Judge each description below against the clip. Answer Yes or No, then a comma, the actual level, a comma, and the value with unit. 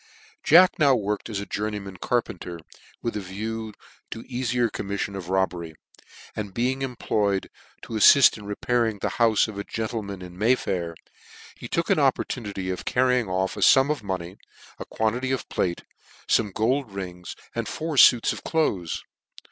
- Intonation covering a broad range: No, average, 4.3 semitones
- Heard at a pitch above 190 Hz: No, low, 105 Hz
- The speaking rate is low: No, average, 170 wpm